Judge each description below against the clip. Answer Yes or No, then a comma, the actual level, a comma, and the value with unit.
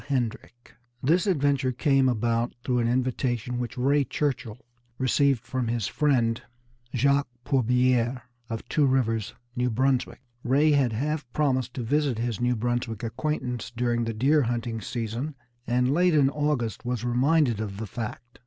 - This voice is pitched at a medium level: No, low, 125 Hz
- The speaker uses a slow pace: No, average, 150 wpm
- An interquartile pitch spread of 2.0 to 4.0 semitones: Yes, average, 2.9 semitones